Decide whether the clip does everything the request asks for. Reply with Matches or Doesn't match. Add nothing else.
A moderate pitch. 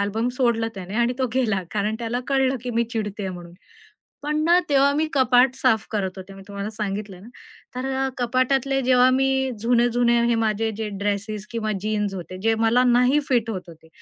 Doesn't match